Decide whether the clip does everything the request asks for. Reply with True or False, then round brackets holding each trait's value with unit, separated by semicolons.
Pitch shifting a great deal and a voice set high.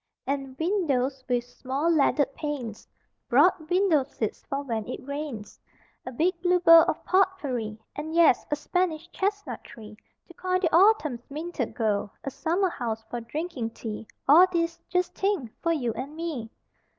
True (5.8 semitones; 295 Hz)